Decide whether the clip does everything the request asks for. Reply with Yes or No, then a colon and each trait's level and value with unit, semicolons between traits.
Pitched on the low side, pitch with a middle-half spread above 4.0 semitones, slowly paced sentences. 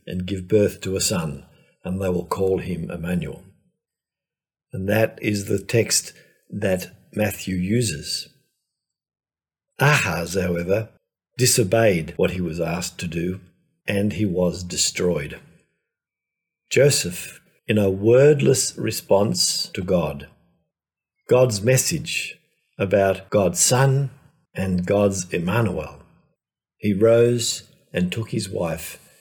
Yes: low, 100 Hz; average, 4.4 semitones; slow, 110 wpm